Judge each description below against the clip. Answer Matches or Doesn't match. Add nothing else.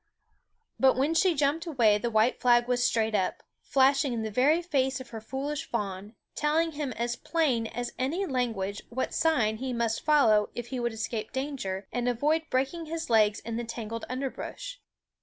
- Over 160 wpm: Matches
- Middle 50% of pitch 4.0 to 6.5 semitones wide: Matches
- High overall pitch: Matches